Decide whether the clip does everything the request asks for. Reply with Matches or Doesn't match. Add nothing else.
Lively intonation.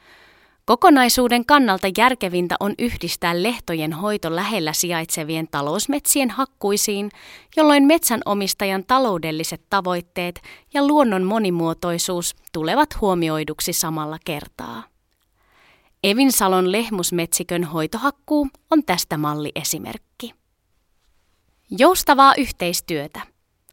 Matches